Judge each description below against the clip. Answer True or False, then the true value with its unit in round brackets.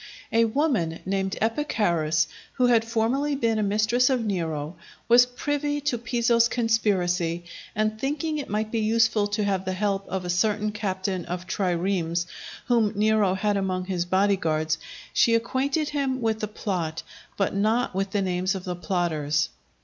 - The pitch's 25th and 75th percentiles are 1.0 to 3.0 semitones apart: False (4.0 semitones)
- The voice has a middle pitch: False (210 Hz)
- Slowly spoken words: False (165 wpm)